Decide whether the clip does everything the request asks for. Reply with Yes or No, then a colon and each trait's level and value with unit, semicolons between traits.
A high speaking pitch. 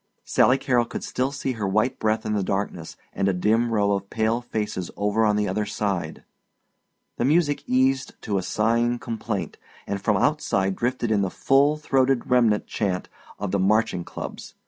No: low, 110 Hz